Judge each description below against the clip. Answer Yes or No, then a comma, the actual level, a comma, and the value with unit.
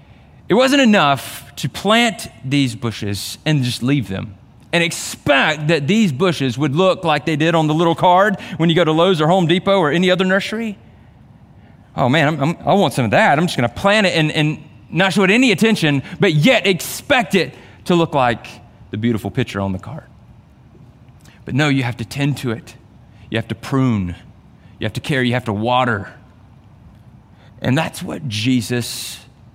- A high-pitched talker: No, low, 135 Hz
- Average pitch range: No, wide, 6.8 semitones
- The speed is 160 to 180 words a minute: No, average, 195 wpm